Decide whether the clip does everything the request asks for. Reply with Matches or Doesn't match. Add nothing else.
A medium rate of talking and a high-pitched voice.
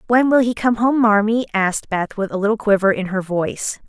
Doesn't match